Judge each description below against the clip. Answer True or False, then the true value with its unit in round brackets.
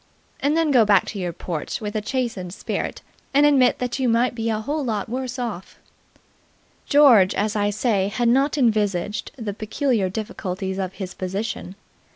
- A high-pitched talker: True (215 Hz)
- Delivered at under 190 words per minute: True (175 wpm)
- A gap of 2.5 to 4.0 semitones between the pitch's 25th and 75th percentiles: False (4.4 semitones)